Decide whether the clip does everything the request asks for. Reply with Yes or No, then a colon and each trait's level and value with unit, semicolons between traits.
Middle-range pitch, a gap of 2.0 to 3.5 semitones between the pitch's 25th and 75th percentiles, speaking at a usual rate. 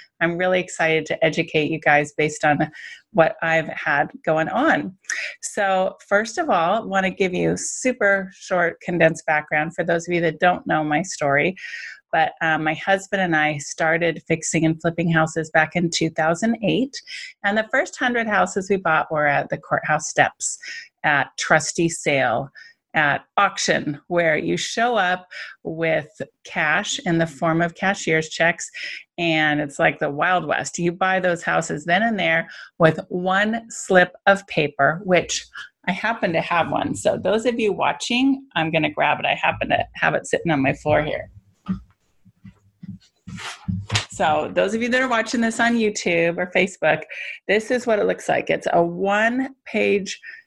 No: medium, 175 Hz; average, 4.3 semitones; average, 170 wpm